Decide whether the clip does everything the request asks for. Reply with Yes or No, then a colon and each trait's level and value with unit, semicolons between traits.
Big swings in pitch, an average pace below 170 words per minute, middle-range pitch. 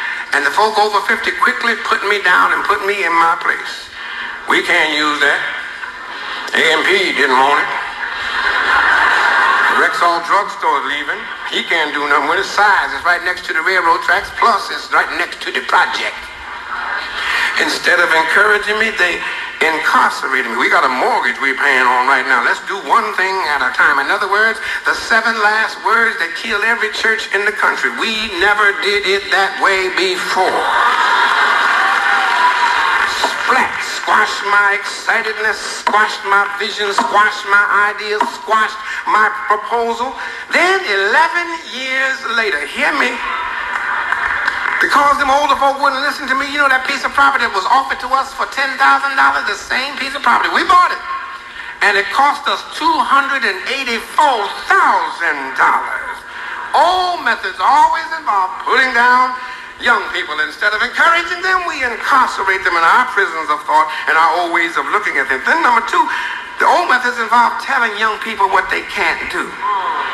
No: wide, 8.8 semitones; average, 160 wpm; high, 245 Hz